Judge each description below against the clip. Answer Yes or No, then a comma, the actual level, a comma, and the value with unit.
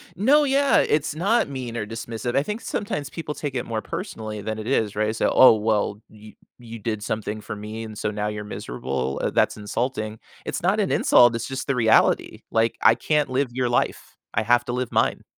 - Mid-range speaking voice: No, low, 115 Hz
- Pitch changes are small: No, average, 3.7 semitones